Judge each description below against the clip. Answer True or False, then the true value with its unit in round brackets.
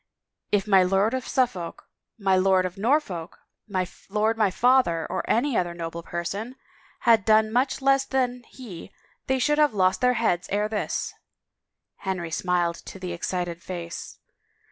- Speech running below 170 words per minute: True (160 wpm)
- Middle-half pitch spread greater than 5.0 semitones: True (5.5 semitones)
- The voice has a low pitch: False (195 Hz)